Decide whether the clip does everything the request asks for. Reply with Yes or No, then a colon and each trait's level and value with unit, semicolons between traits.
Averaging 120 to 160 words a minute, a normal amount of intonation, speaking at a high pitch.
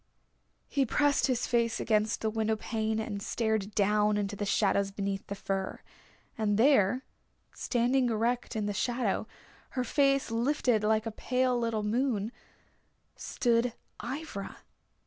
Yes: slow, 135 wpm; average, 3.0 semitones; high, 220 Hz